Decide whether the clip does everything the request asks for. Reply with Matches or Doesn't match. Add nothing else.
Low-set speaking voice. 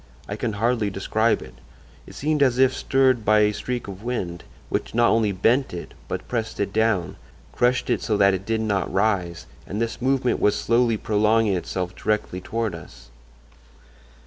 Matches